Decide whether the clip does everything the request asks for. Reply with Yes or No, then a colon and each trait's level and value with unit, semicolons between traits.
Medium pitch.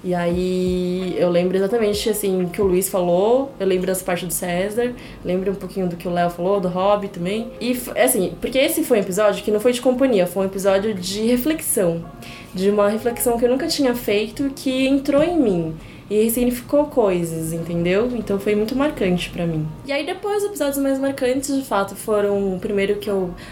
No: high, 205 Hz